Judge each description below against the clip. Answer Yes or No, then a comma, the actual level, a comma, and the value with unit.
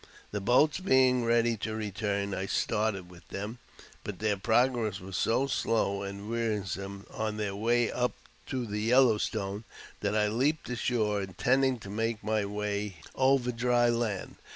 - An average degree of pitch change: Yes, average, 3.1 semitones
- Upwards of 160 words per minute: No, average, 155 wpm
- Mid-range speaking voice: No, low, 110 Hz